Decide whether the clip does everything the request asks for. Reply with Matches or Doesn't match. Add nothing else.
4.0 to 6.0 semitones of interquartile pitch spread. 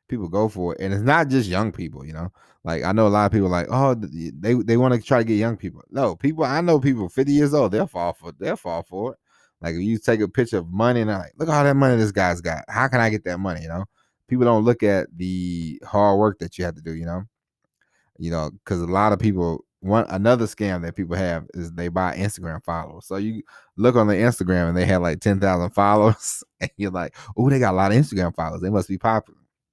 Matches